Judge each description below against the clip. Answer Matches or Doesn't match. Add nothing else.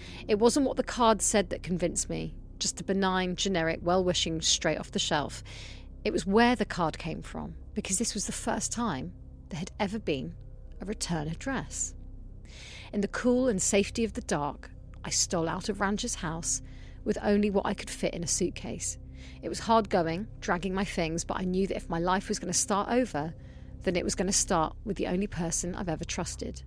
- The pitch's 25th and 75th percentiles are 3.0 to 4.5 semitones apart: Doesn't match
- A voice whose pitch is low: Doesn't match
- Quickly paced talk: Matches